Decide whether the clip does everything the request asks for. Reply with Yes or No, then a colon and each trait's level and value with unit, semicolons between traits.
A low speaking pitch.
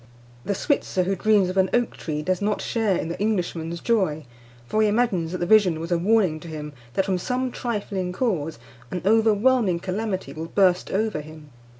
No: high, 190 Hz